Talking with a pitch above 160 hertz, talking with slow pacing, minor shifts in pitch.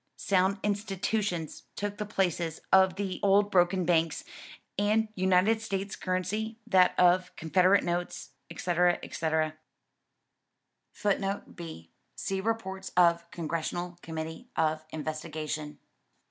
No: medium, 185 Hz; slow, 105 wpm; average, 3.2 semitones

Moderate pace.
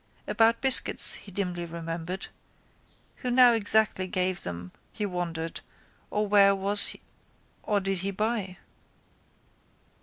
No: slow, 115 wpm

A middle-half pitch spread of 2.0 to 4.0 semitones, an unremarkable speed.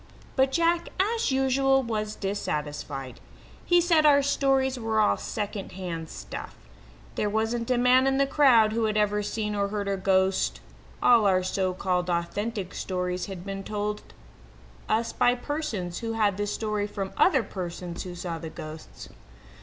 No: average, 5.1 semitones; average, 160 wpm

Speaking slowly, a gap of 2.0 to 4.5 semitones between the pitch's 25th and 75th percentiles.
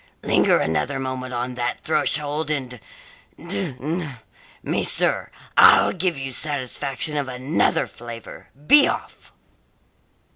Yes: slow, 115 wpm; average, 3.4 semitones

